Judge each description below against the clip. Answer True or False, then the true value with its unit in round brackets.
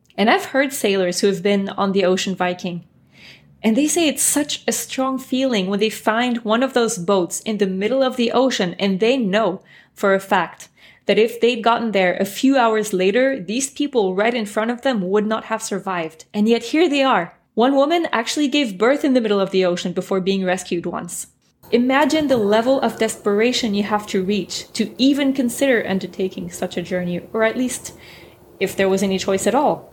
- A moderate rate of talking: False (210 wpm)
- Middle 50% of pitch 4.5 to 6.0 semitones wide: True (4.8 semitones)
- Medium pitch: False (220 Hz)